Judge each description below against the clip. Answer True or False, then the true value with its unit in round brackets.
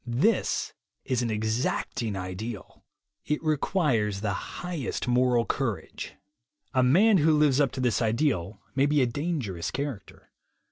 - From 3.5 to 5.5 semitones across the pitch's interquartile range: True (5.2 semitones)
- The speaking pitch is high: False (125 Hz)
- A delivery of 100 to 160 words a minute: True (135 wpm)